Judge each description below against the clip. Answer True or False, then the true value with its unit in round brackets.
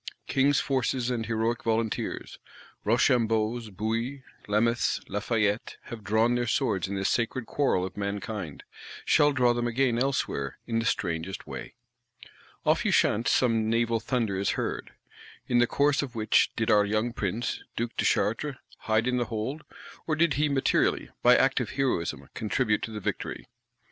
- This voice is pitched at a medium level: False (115 Hz)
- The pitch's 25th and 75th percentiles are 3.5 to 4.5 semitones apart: False (2.8 semitones)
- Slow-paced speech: False (155 wpm)